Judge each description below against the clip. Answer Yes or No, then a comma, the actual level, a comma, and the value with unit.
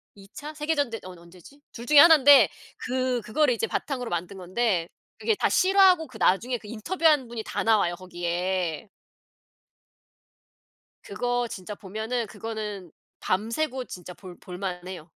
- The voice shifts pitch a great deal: Yes, wide, 6.1 semitones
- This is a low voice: No, high, 225 Hz